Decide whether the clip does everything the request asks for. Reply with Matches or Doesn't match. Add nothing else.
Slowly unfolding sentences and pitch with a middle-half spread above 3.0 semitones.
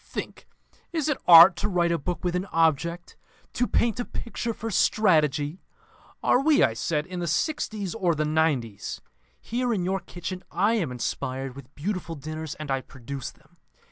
Doesn't match